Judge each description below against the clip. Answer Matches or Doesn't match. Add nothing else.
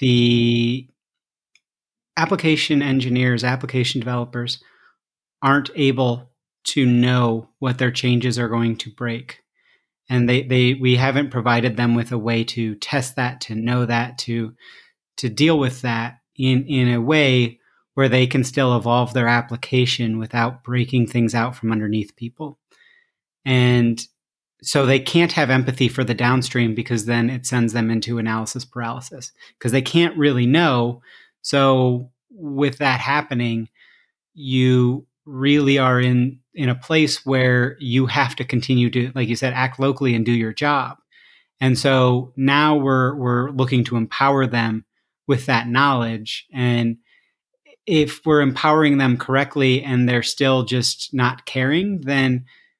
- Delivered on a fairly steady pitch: Matches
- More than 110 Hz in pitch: Matches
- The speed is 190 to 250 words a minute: Doesn't match